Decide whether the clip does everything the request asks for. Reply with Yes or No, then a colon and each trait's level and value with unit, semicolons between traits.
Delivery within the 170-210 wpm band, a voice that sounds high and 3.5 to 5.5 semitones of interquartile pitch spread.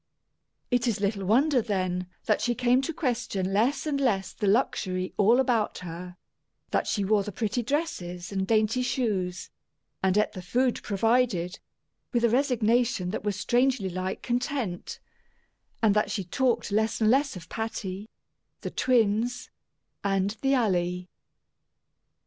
No: average, 145 wpm; high, 215 Hz; average, 4.5 semitones